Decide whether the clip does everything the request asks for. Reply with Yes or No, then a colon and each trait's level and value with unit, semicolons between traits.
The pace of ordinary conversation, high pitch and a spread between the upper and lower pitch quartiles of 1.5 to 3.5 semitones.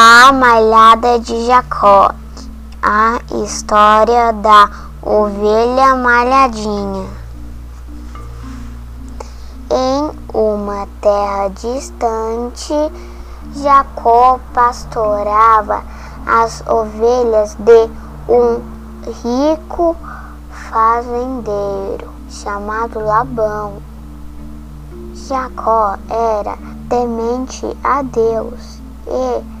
No: slow, 60 wpm; high, 225 Hz; average, 3.2 semitones